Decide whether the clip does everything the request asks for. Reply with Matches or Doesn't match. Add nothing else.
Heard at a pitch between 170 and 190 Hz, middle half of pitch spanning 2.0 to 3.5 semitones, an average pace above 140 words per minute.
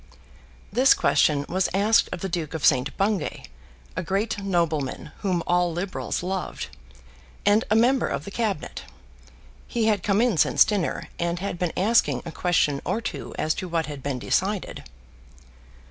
Doesn't match